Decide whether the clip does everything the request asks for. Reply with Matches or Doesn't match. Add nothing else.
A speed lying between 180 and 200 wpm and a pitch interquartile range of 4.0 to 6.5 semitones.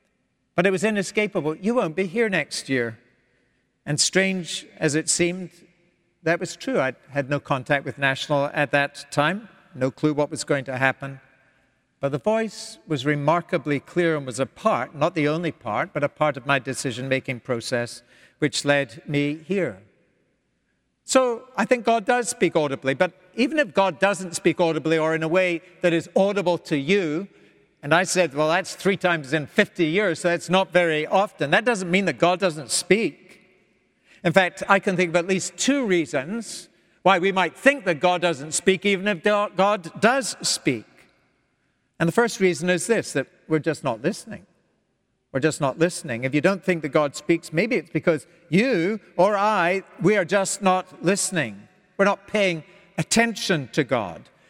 Matches